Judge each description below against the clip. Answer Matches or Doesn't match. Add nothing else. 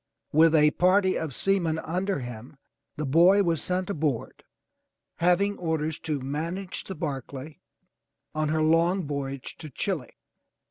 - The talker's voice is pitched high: Doesn't match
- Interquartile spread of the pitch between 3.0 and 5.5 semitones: Matches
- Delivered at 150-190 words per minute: Doesn't match